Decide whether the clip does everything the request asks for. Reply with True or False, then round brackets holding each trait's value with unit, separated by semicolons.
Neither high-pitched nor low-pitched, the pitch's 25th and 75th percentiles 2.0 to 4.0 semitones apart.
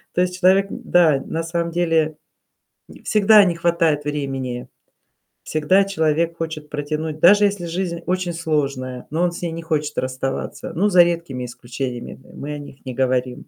True (160 Hz; 3.7 semitones)